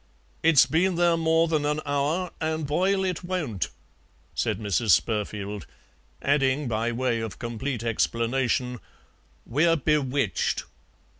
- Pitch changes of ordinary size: No, wide, 5.7 semitones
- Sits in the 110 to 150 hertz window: Yes, medium, 140 Hz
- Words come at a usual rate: No, slow, 120 wpm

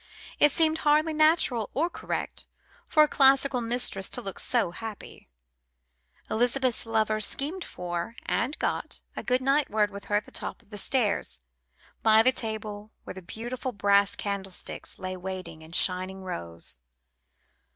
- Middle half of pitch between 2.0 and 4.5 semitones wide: No, wide, 5.5 semitones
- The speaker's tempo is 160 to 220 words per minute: No, average, 150 wpm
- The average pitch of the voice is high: Yes, high, 220 Hz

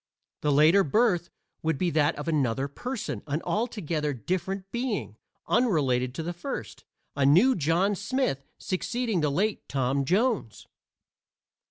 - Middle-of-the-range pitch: Yes, medium, 170 Hz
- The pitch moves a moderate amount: No, wide, 6.7 semitones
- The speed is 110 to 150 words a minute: Yes, average, 140 wpm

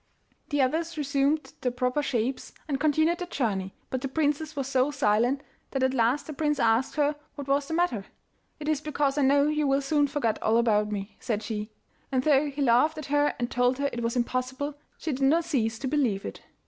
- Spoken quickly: Yes, fast, 215 wpm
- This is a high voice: Yes, very high, 275 Hz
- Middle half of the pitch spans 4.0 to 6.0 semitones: No, average, 3.3 semitones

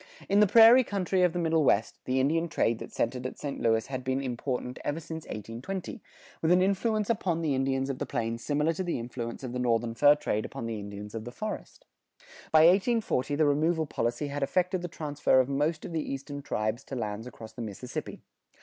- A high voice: No, medium, 140 Hz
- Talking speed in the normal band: No, fast, 215 wpm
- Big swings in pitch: Yes, wide, 6.0 semitones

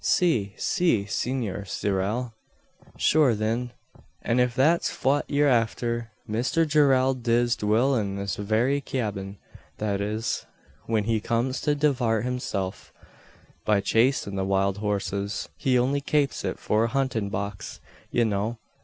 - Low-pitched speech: Yes, low, 115 Hz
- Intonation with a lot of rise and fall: No, average, 4.3 semitones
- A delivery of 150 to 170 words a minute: No, slow, 135 wpm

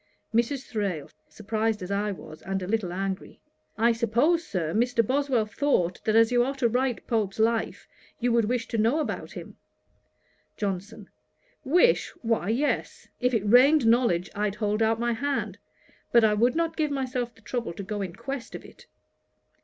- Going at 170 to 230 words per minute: Yes, average, 175 wpm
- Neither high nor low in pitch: No, high, 225 Hz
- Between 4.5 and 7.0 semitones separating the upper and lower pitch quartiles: No, average, 3.3 semitones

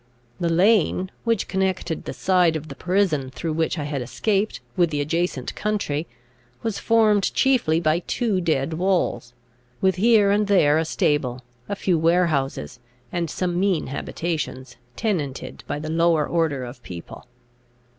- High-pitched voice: No, medium, 170 Hz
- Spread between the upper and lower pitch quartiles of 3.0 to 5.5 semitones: Yes, average, 4.6 semitones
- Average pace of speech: Yes, average, 150 wpm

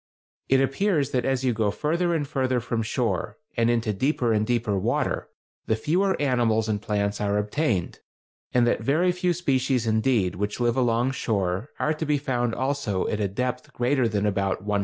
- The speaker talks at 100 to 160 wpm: No, average, 190 wpm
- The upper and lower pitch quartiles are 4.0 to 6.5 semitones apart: Yes, average, 4.5 semitones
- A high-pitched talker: No, low, 120 Hz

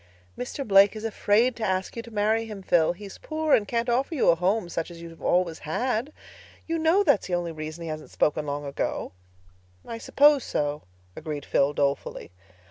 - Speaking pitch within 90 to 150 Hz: No, high, 195 Hz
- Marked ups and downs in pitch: Yes, wide, 6.5 semitones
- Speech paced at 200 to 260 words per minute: Yes, fast, 205 wpm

